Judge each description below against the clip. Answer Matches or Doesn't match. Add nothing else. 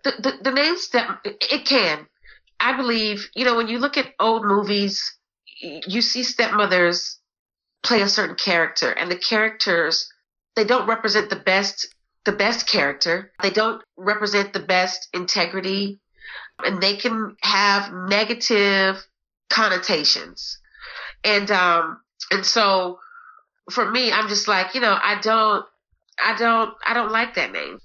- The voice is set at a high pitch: Matches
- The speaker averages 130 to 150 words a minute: Matches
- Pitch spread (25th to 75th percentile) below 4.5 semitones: Matches